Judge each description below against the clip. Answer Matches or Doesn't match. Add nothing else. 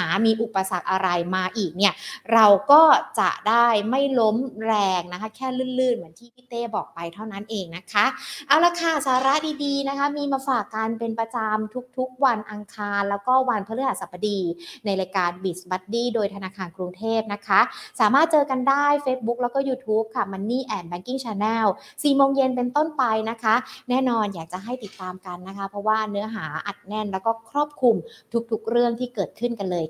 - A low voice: Doesn't match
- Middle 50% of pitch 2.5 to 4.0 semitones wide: Doesn't match